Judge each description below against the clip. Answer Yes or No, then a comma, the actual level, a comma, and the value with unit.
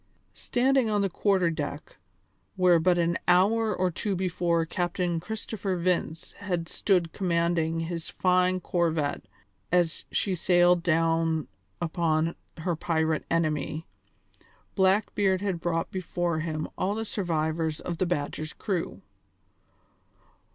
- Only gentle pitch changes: Yes, narrow, 2.3 semitones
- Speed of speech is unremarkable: No, slow, 120 wpm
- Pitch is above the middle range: No, medium, 175 Hz